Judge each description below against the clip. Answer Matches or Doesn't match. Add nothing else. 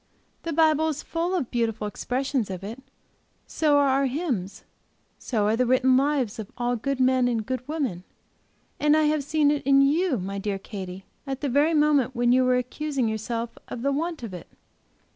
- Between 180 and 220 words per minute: Matches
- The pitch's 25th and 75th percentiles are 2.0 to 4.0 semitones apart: Doesn't match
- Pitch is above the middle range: Matches